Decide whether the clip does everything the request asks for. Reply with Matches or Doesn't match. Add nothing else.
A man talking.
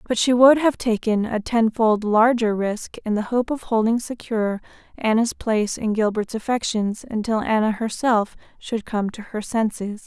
Doesn't match